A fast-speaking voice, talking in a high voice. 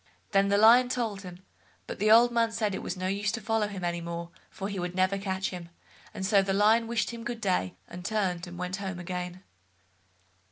Yes: fast, 225 wpm; high, 195 Hz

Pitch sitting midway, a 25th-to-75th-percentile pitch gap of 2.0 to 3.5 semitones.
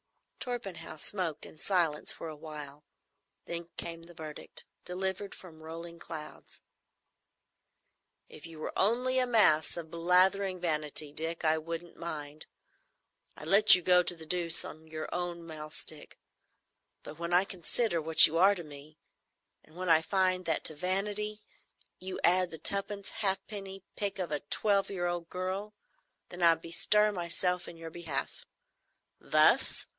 Yes: medium, 170 Hz; average, 3.2 semitones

